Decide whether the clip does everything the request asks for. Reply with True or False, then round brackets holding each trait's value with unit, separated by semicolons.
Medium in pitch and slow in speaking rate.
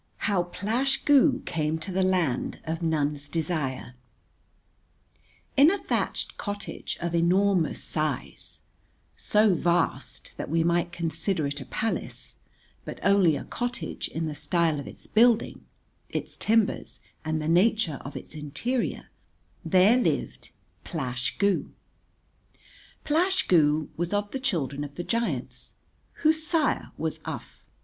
True (175 Hz; 130 wpm)